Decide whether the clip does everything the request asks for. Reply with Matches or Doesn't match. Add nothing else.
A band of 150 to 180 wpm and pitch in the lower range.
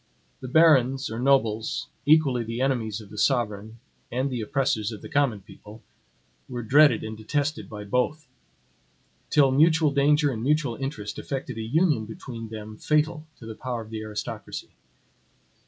Matches